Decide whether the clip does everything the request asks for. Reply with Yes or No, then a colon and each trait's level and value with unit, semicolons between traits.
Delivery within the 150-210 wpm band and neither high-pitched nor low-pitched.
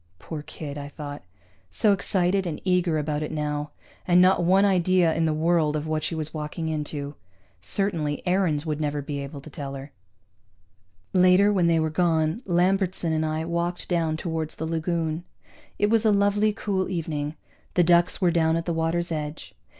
Yes: average, 180 wpm; medium, 165 Hz